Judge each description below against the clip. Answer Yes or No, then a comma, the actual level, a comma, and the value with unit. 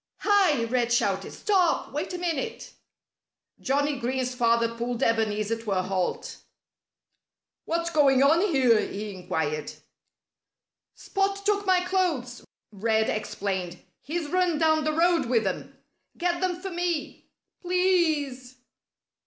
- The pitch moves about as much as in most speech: No, wide, 7.4 semitones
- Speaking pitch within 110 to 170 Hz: No, very high, 280 Hz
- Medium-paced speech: No, slow, 120 wpm